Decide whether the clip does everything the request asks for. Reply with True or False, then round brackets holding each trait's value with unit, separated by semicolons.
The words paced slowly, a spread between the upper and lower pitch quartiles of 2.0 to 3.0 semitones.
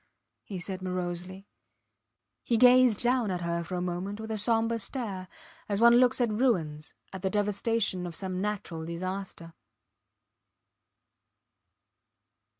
False (130 wpm; 4.1 semitones)